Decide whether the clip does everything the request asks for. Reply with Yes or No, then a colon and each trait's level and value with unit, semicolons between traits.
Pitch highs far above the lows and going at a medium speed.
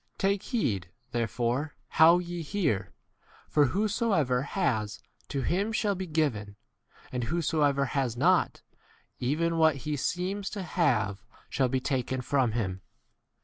No: wide, 6.3 semitones; slow, 130 wpm